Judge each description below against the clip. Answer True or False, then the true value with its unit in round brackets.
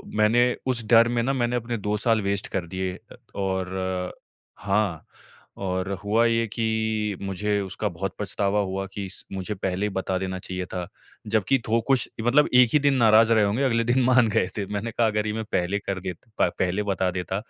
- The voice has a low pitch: True (105 Hz)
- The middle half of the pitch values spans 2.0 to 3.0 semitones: False (3.5 semitones)